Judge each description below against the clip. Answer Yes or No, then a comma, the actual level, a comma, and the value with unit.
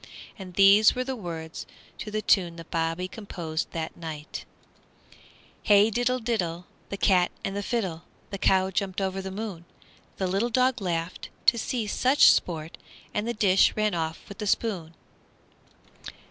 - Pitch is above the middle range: Yes, high, 195 Hz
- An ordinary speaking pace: Yes, average, 160 wpm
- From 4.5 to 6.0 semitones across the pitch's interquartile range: No, average, 4.0 semitones